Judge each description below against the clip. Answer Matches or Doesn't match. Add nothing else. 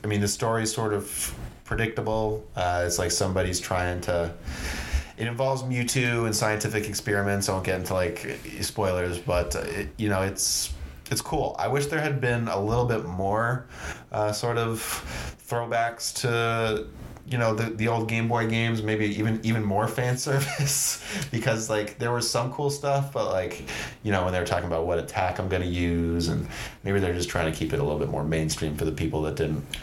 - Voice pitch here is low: Matches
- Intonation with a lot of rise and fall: Doesn't match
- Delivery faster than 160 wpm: Matches